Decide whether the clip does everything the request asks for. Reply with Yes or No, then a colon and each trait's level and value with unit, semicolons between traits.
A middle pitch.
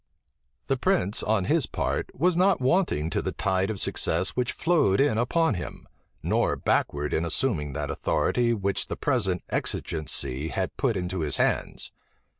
No: low, 105 Hz